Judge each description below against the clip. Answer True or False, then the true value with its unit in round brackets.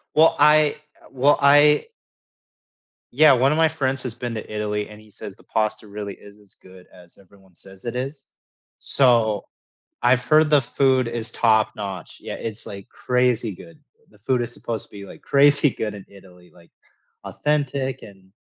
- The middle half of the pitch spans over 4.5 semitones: True (5.2 semitones)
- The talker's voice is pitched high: False (115 Hz)